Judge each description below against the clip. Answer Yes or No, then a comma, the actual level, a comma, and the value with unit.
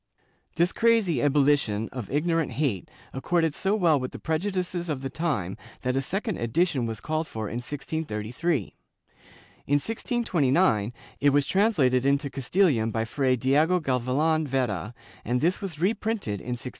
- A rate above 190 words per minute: No, average, 155 wpm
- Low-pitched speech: No, medium, 145 Hz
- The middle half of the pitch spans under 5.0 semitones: No, wide, 5.5 semitones